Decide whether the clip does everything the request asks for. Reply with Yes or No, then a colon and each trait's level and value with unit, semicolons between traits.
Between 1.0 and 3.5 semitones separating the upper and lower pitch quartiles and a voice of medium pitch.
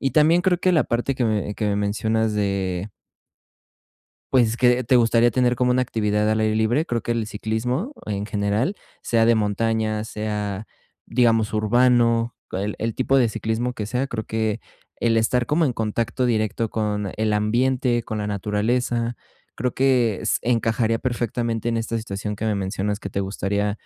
No: narrow, 2.6 semitones; low, 110 Hz